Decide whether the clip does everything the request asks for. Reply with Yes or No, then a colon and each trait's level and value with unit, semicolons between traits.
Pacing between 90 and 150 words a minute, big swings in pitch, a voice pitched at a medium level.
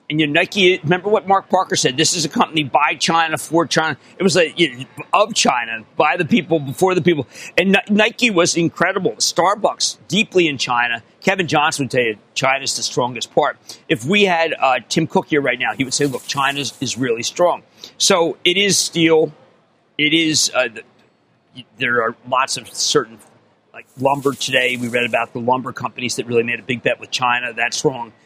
No: average, 200 wpm; wide, 5.7 semitones; medium, 155 Hz